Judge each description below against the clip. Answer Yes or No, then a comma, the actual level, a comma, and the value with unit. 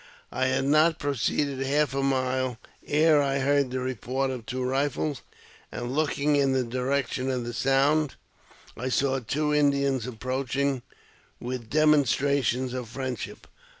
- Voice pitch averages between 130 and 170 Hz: Yes, low, 135 Hz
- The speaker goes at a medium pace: Yes, average, 145 wpm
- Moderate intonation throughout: No, narrow, 1.8 semitones